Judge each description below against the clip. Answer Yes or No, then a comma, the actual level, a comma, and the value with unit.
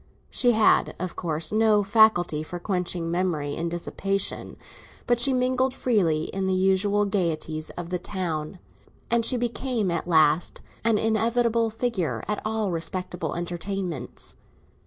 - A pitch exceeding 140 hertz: Yes, high, 190 Hz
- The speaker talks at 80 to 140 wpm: Yes, slow, 135 wpm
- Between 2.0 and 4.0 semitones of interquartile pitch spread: No, average, 4.6 semitones